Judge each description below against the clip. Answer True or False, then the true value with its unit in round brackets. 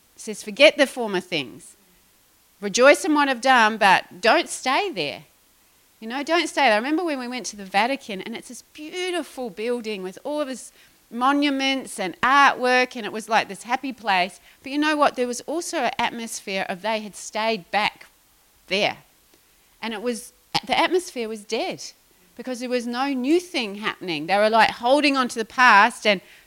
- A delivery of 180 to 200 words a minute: True (195 wpm)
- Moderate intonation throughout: True (4.6 semitones)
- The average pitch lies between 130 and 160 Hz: False (245 Hz)